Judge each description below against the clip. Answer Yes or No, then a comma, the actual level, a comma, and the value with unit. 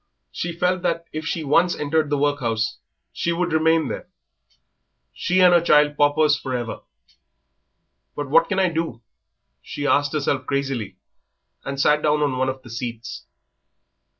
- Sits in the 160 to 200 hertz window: No, medium, 150 Hz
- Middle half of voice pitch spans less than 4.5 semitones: Yes, average, 3.7 semitones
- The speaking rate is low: No, average, 155 wpm